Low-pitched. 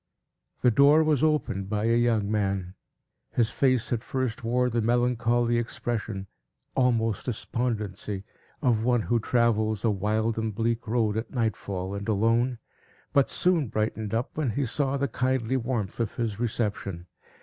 Yes: low, 115 Hz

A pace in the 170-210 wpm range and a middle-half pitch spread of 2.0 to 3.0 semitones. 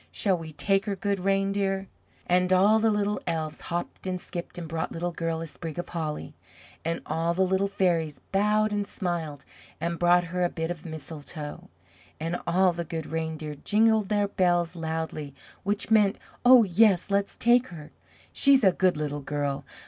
No: average, 175 wpm; average, 3.5 semitones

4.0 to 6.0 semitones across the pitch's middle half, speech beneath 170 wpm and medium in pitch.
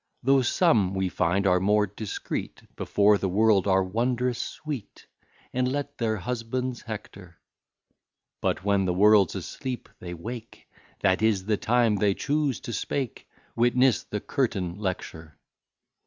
No: average, 4.4 semitones; average, 140 wpm; low, 105 Hz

